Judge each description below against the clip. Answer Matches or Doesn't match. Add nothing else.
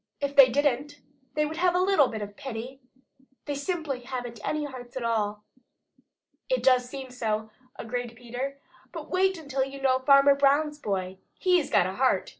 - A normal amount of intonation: Matches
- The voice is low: Doesn't match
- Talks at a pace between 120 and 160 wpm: Doesn't match